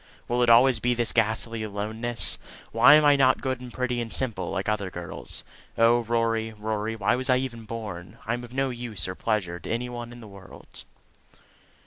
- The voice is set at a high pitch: No, low, 115 Hz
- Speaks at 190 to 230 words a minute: Yes, fast, 205 wpm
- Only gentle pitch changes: Yes, narrow, 2.3 semitones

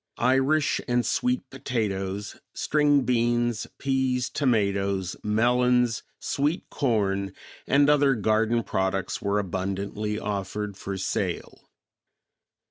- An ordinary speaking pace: No, slow, 95 wpm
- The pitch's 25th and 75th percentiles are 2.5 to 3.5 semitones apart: No, average, 4.6 semitones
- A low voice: Yes, low, 115 Hz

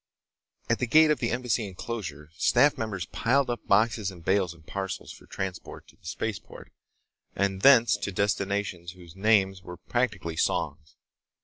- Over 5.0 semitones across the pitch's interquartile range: No, average, 4.6 semitones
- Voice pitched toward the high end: No, low, 100 Hz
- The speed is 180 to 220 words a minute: No, average, 155 wpm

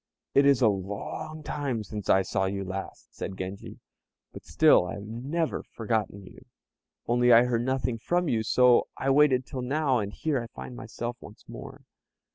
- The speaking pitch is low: Yes, low, 120 Hz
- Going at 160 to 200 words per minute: Yes, average, 180 wpm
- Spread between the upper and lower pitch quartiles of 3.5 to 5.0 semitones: Yes, average, 4.7 semitones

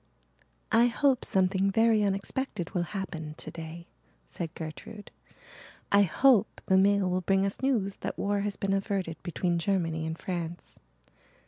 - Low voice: No, high, 195 Hz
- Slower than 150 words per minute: Yes, average, 140 wpm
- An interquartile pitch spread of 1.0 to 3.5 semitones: Yes, average, 2.9 semitones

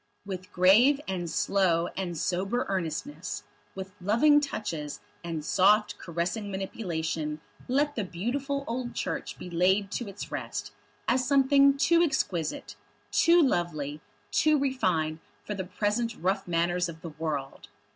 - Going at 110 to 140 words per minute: Yes, slow, 135 wpm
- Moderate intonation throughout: No, wide, 6.4 semitones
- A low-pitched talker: No, high, 190 Hz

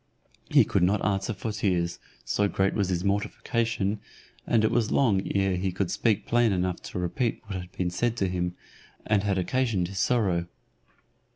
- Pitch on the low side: Yes, low, 100 Hz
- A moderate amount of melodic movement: Yes, average, 3.3 semitones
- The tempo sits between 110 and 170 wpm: No, average, 180 wpm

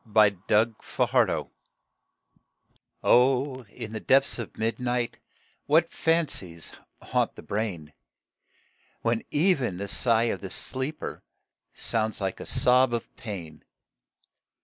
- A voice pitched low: Yes, low, 115 Hz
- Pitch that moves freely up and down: No, average, 4.1 semitones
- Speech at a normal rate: No, slow, 110 wpm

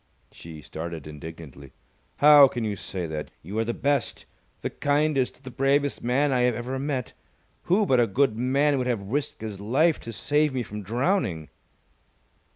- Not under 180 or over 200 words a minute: No, average, 170 wpm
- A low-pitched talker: Yes, low, 125 Hz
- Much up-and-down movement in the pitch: Yes, wide, 6.3 semitones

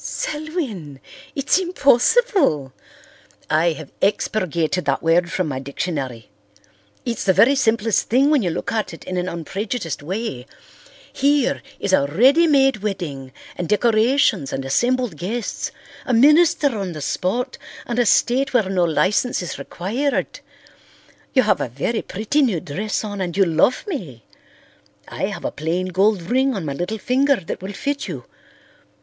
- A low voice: No, high, 200 Hz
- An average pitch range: No, wide, 7.5 semitones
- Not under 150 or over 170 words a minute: Yes, average, 155 wpm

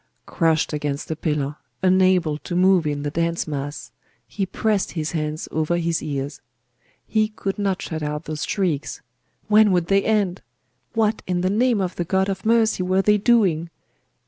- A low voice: No, medium, 180 Hz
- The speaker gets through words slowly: No, average, 170 wpm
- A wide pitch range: No, average, 4.2 semitones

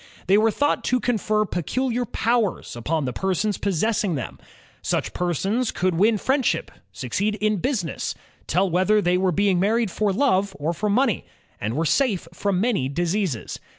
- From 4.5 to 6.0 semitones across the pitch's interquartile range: No, average, 4.1 semitones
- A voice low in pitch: No, high, 200 Hz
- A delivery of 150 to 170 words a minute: Yes, average, 160 wpm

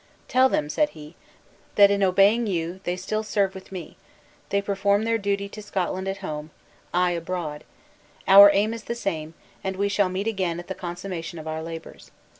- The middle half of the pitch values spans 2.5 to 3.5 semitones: Yes, average, 2.8 semitones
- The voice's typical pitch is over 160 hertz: Yes, high, 190 Hz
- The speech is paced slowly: No, average, 190 wpm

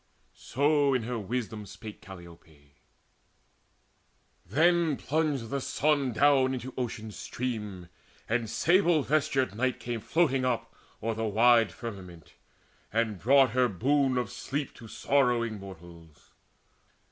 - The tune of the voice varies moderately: Yes, average, 4.6 semitones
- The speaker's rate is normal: No, slow, 120 wpm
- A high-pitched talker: No, low, 120 Hz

